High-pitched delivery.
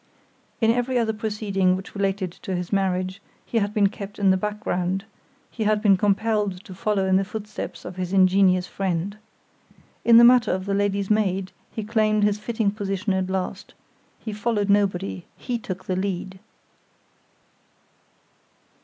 Yes: high, 200 Hz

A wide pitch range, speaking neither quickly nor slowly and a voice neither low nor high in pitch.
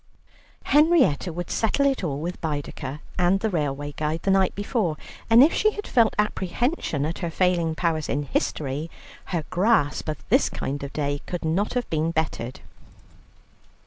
Yes: wide, 5.8 semitones; average, 165 wpm; medium, 170 Hz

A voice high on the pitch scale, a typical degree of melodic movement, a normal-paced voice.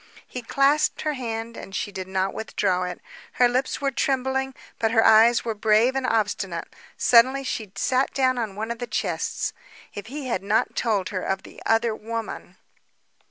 Yes: high, 230 Hz; average, 3.7 semitones; average, 180 wpm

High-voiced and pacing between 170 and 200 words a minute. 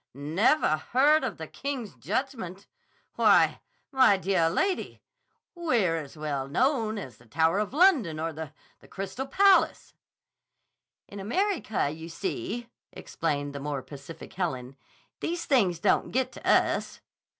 No: high, 195 Hz; slow, 135 wpm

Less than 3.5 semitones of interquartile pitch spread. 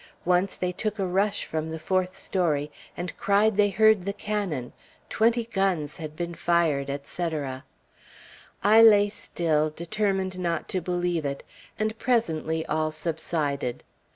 No: average, 4.4 semitones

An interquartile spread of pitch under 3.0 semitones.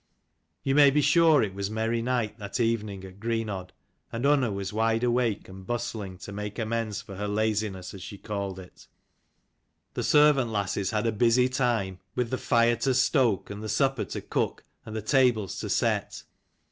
No: average, 3.5 semitones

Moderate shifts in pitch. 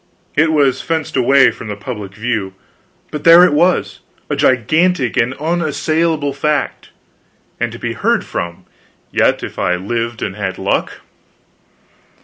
No: wide, 6.9 semitones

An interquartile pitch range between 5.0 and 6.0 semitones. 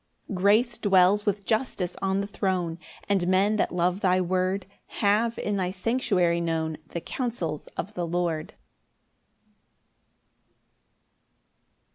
No: average, 2.7 semitones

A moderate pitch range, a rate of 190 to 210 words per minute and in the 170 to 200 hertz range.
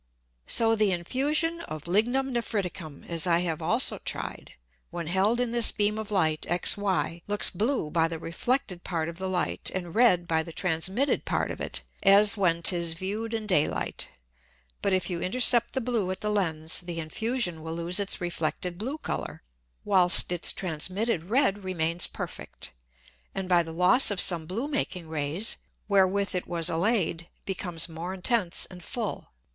No: average, 4.2 semitones; average, 170 wpm; medium, 185 Hz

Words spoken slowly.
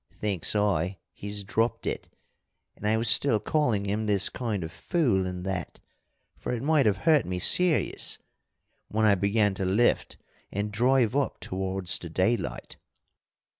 No: average, 155 wpm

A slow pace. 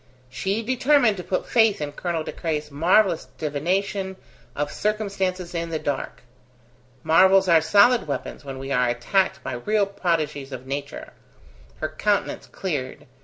No: average, 145 wpm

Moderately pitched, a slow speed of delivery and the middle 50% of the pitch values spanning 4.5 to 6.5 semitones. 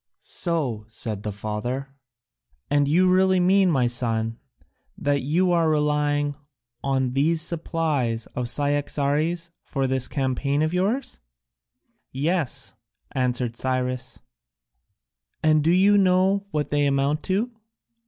Yes: medium, 145 Hz; slow, 120 wpm; average, 4.8 semitones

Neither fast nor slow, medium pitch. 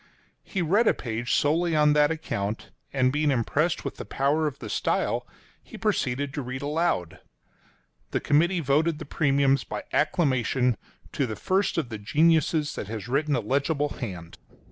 Yes: average, 170 wpm; medium, 145 Hz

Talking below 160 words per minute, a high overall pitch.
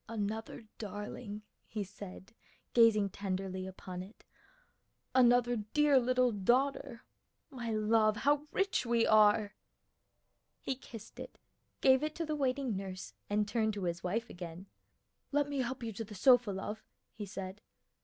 Yes: average, 145 wpm; high, 220 Hz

